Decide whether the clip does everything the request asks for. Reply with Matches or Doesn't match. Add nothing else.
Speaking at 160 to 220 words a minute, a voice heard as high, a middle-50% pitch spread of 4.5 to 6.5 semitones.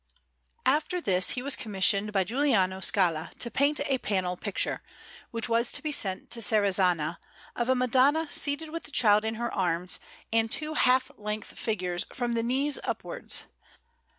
Matches